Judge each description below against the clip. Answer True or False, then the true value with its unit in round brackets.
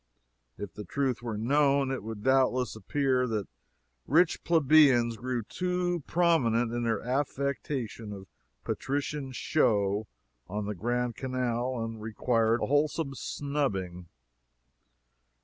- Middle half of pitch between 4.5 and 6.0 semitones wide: False (4.0 semitones)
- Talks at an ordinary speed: False (115 wpm)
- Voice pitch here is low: True (125 Hz)